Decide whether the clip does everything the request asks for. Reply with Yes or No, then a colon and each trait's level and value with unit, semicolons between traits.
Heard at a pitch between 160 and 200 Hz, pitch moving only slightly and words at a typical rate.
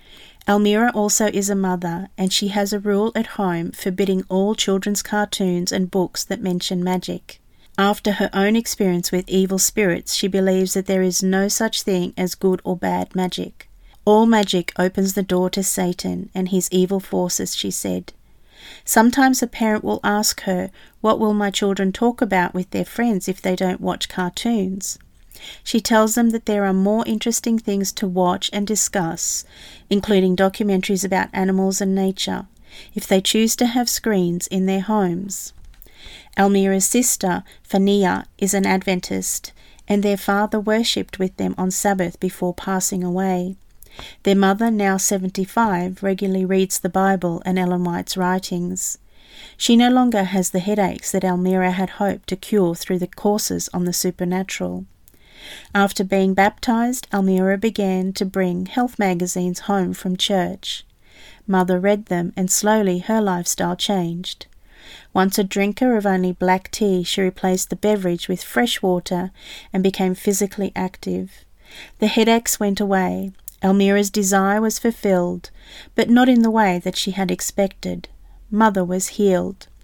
Yes: high, 190 Hz; narrow, 2.0 semitones; average, 155 wpm